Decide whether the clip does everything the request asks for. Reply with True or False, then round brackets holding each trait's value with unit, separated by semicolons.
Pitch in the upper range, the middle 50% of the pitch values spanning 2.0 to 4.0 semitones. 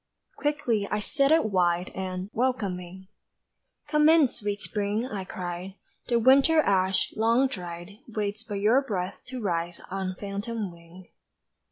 False (205 Hz; 4.6 semitones)